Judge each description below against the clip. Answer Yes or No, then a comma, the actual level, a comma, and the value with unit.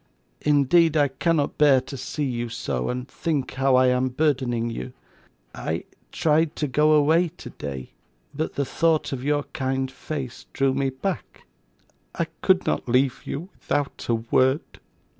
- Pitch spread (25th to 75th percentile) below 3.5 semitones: Yes, average, 3.0 semitones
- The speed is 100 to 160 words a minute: Yes, average, 155 wpm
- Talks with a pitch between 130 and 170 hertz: Yes, low, 135 Hz